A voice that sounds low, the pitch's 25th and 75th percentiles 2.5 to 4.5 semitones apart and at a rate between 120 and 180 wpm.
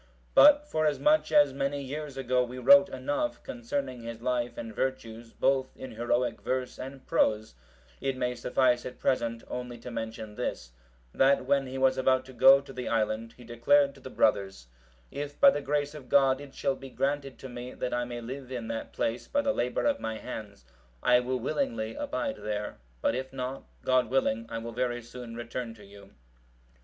No: low, 125 Hz; average, 2.9 semitones; average, 190 wpm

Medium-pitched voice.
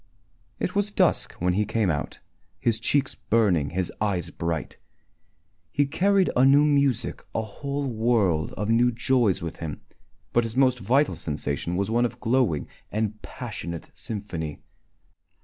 No: low, 110 Hz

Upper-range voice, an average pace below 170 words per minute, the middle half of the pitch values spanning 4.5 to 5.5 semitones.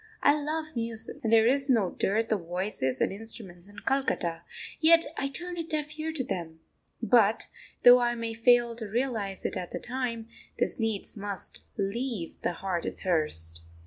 No: high, 225 Hz; average, 175 wpm; average, 5.2 semitones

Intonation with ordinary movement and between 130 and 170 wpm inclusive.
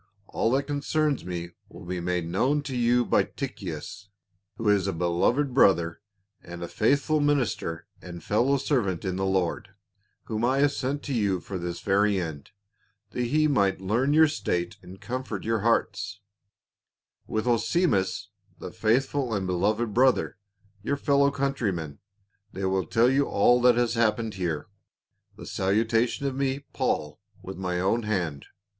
No: wide, 6.0 semitones; average, 160 wpm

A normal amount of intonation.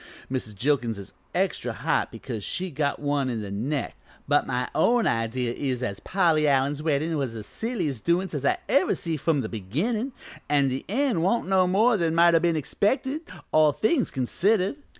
No: wide, 6.3 semitones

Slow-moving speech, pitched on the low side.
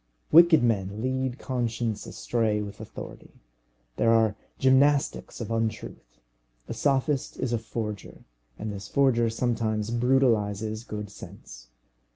Yes: slow, 120 wpm; low, 115 Hz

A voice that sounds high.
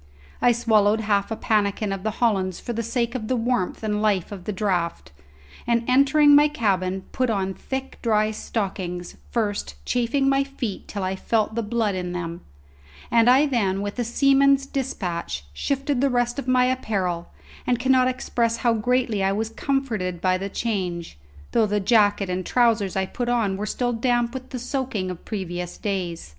Yes: high, 220 Hz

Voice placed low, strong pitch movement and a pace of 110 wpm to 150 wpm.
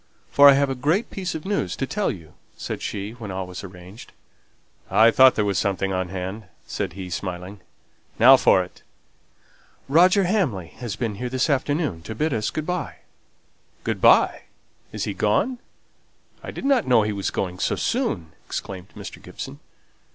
No: low, 110 Hz; wide, 7.3 semitones; average, 175 wpm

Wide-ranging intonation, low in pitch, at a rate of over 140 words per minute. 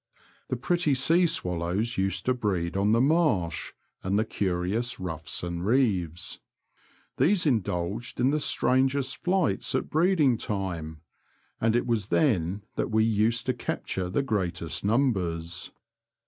No: wide, 6.6 semitones; low, 110 Hz; slow, 135 wpm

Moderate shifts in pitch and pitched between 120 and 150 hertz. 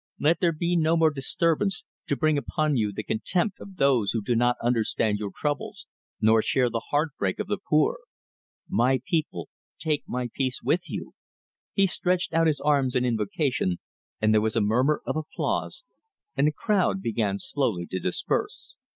No: wide, 6.1 semitones; medium, 140 Hz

